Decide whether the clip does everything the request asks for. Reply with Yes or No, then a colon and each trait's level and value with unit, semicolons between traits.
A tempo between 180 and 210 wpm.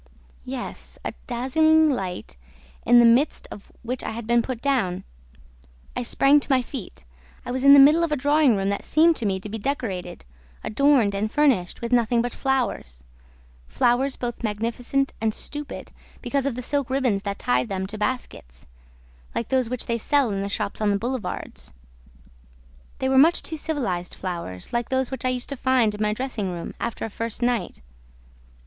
Yes: average, 185 wpm